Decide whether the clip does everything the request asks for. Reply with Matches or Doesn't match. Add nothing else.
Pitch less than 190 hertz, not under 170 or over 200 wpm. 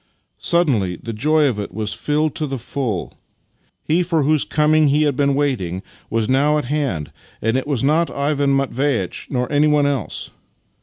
Matches